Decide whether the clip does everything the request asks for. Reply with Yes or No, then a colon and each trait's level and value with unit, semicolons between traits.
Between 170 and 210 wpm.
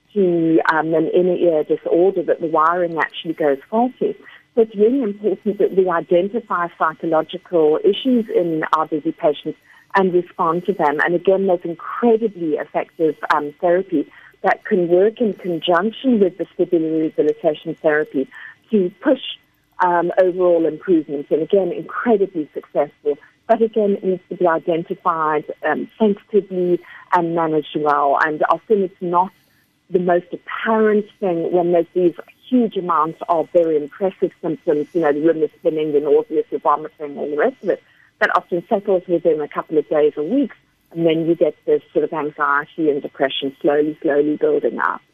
No: average, 160 wpm